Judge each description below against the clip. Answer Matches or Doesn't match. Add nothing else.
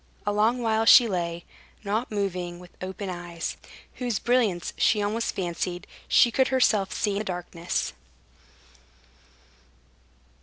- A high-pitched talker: Matches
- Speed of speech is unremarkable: Doesn't match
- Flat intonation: Doesn't match